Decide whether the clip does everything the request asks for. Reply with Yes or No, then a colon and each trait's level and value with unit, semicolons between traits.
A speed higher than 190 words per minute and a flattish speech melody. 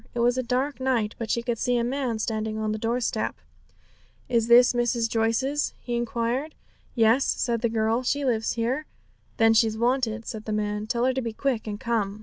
Yes: average, 200 wpm; narrow, 2.1 semitones